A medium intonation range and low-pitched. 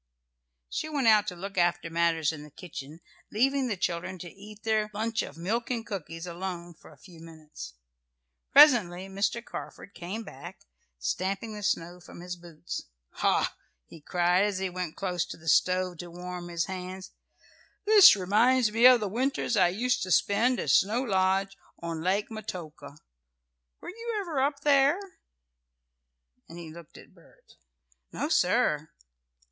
No: average, 4.5 semitones; medium, 185 Hz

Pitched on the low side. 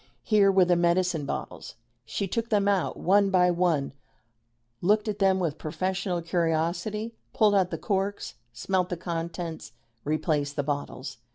No: medium, 180 Hz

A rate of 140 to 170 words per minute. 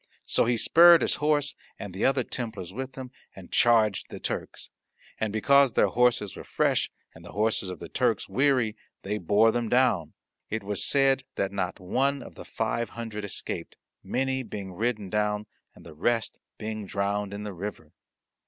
No: average, 180 wpm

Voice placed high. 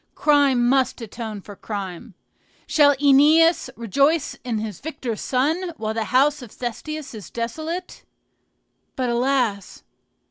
Yes: very high, 255 Hz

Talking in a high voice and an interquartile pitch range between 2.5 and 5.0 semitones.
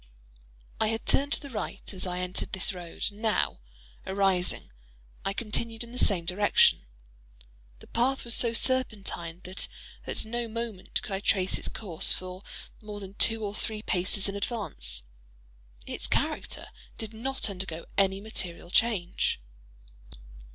Yes: high, 200 Hz; average, 3.6 semitones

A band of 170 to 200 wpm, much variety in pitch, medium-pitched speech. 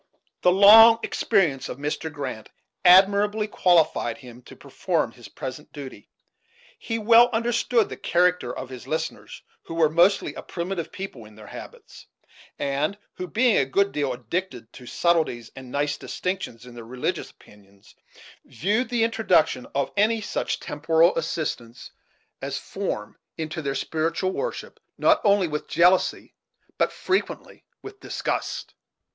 No: average, 140 wpm; wide, 7.2 semitones; medium, 165 Hz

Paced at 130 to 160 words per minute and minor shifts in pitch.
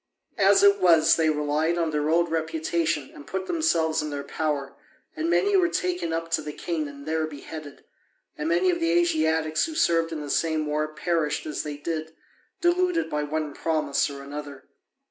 No: average, 185 wpm; narrow, 2.3 semitones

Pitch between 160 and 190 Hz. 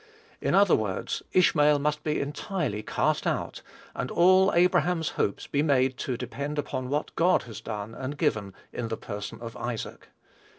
No: medium, 140 Hz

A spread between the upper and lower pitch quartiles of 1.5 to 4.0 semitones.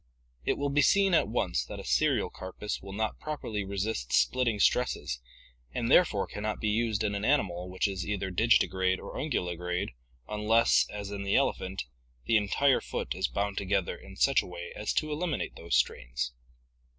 Yes: average, 3.7 semitones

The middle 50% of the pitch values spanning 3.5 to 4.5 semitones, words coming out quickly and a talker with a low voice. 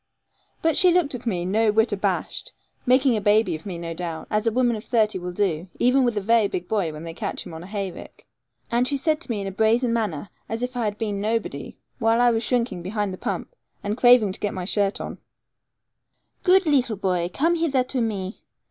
No: average, 4.2 semitones; fast, 230 wpm; high, 220 Hz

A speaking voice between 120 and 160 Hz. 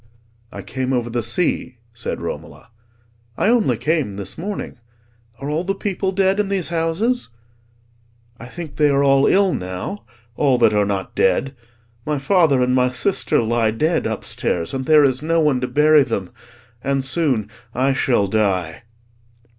Yes: low, 135 Hz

